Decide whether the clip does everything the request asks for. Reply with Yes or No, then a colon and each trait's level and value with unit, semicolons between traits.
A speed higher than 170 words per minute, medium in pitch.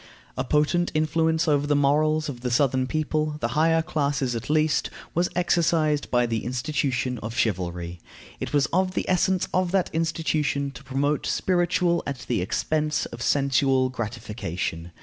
No: average, 155 wpm; medium, 145 Hz